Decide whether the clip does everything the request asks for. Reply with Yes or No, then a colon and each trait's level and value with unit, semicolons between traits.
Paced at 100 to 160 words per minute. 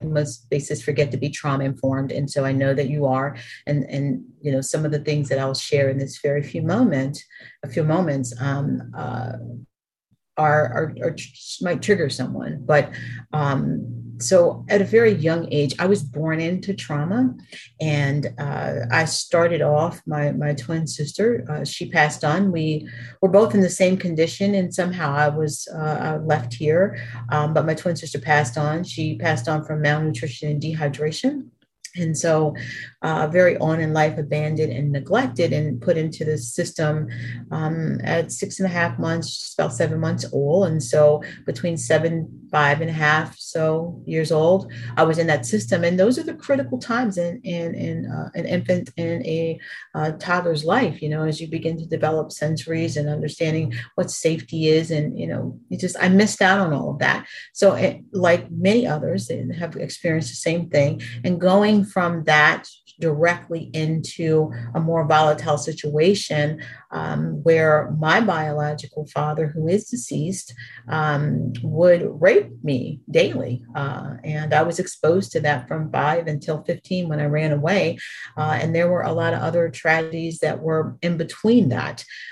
No: average, 175 wpm